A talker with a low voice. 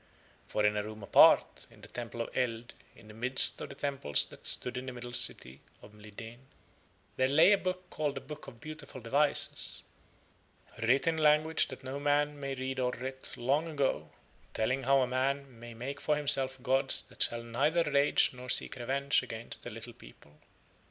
Yes: low, 130 Hz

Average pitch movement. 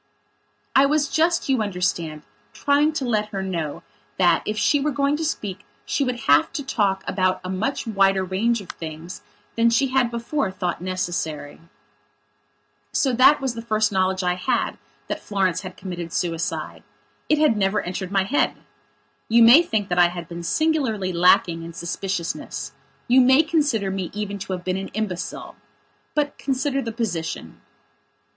No: wide, 6.2 semitones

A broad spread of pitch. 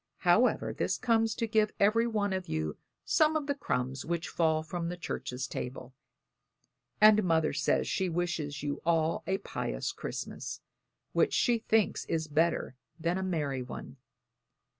Yes: wide, 6.4 semitones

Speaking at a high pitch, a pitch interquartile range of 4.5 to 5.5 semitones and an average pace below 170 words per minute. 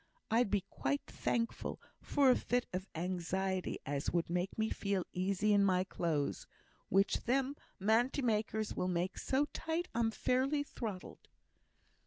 Yes: high, 200 Hz; average, 5.0 semitones; average, 145 wpm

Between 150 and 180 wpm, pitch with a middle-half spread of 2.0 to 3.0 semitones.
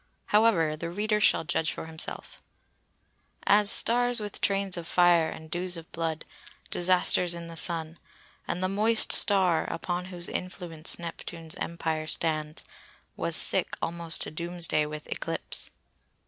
No: average, 140 wpm; narrow, 2.4 semitones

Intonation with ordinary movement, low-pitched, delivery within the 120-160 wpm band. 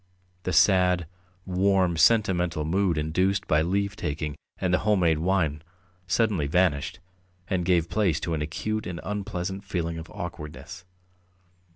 Yes: average, 3.2 semitones; very low, 90 Hz; average, 140 wpm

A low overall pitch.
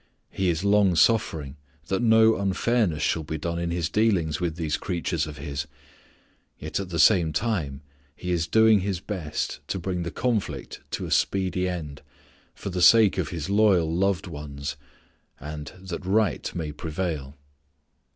Yes: very low, 90 Hz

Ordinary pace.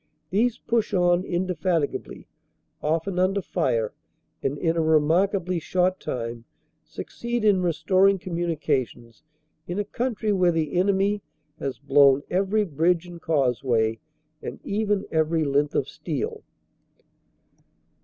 No: slow, 120 wpm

